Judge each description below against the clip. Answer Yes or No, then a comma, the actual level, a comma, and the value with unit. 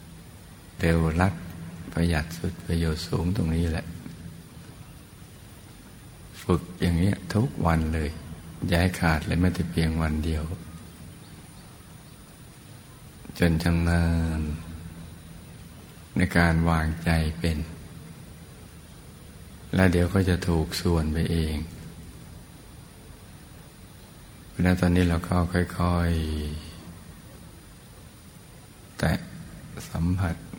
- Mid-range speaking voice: No, very low, 85 Hz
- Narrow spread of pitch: Yes, narrow, 1.2 semitones